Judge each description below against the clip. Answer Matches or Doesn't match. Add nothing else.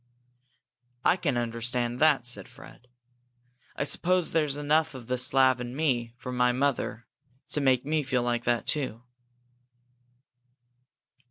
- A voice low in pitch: Matches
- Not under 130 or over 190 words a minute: Matches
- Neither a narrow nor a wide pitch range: Matches